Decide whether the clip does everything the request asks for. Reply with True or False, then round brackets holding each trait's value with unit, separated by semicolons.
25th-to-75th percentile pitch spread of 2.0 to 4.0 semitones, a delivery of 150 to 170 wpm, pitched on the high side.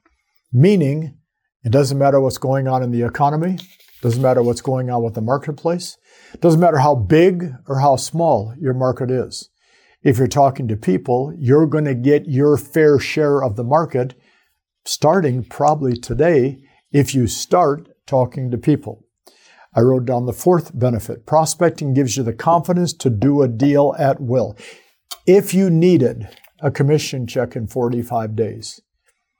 False (3.7 semitones; 160 wpm; 135 Hz)